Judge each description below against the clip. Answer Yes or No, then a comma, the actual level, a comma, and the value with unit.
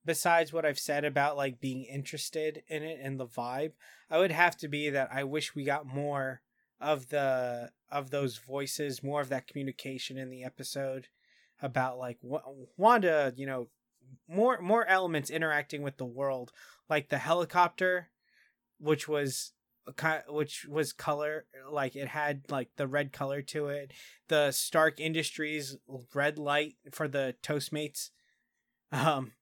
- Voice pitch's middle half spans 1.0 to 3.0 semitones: Yes, narrow, 2.6 semitones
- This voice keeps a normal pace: Yes, average, 155 wpm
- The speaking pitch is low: No, medium, 145 Hz